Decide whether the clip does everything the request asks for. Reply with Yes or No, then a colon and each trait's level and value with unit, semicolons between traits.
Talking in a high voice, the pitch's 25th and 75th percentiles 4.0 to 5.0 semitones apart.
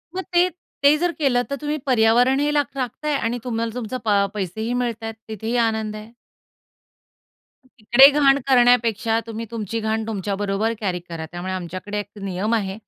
No: high, 225 Hz; average, 3.3 semitones